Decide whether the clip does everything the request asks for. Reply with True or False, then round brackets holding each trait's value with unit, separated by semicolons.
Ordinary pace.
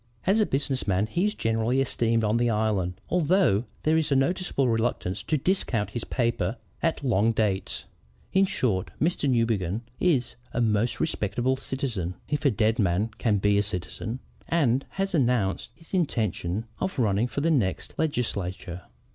True (165 wpm)